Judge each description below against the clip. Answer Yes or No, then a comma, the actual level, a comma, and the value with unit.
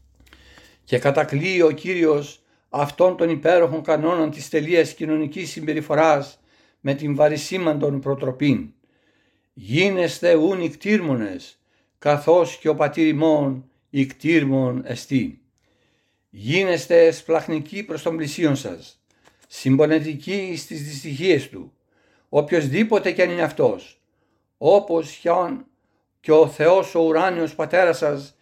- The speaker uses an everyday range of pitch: Yes, average, 3.1 semitones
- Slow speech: Yes, slow, 105 wpm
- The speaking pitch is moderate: Yes, medium, 155 Hz